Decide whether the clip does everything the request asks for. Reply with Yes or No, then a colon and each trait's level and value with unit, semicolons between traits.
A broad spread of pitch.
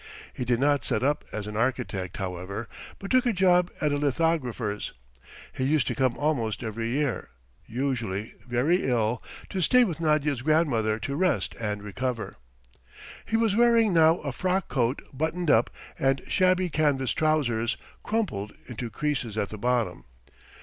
Yes: wide, 6.1 semitones